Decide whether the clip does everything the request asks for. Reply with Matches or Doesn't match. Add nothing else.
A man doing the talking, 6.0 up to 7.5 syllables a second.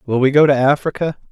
Matches